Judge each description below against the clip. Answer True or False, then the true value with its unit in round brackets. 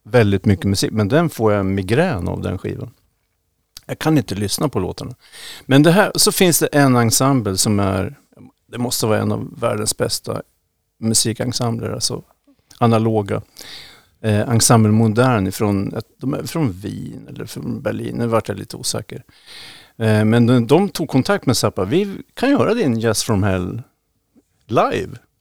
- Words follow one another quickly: False (165 wpm)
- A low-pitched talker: True (115 Hz)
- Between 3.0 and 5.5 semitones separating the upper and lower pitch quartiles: True (4.2 semitones)